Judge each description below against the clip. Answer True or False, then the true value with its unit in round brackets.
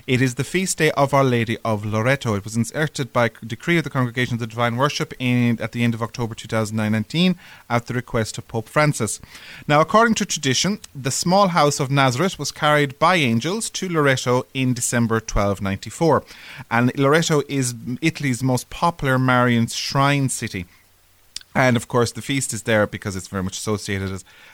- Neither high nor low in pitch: False (125 Hz)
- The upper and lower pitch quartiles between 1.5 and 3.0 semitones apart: False (4.3 semitones)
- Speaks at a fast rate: False (185 wpm)